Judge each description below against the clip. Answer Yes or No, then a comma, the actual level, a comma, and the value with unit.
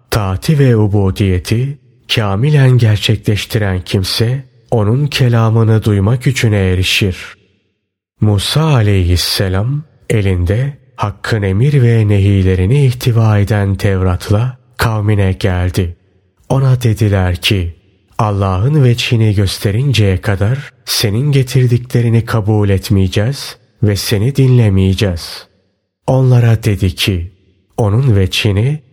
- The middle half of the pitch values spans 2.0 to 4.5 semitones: Yes, average, 4.1 semitones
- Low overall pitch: Yes, low, 105 Hz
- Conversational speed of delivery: No, slow, 85 wpm